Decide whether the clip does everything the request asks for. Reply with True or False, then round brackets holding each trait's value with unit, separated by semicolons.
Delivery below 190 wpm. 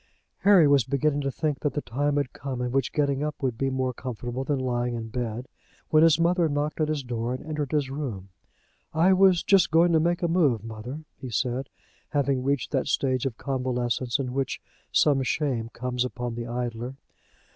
False (200 wpm)